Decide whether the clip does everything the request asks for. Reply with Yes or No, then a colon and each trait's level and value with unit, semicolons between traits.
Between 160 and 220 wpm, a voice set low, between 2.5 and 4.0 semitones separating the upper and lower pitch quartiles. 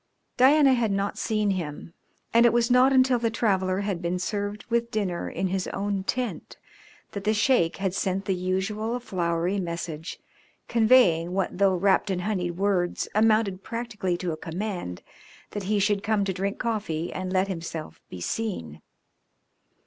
No: average, 165 wpm; high, 195 Hz; average, 3.4 semitones